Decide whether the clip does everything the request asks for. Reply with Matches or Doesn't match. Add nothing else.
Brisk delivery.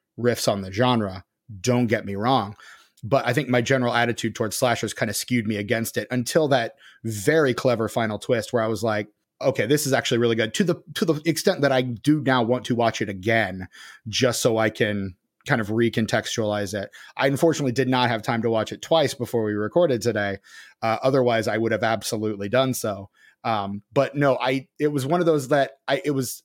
Matches